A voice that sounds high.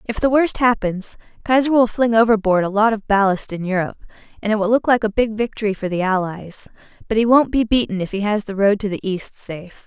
Yes: high, 215 Hz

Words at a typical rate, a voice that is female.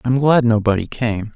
No: average, 180 wpm; male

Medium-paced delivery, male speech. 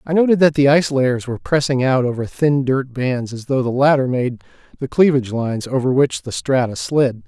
No: fast, 215 wpm; male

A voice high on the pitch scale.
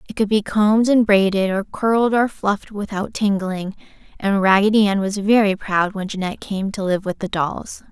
Yes: high, 200 Hz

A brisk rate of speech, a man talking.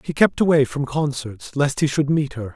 Yes: fast, 235 wpm; male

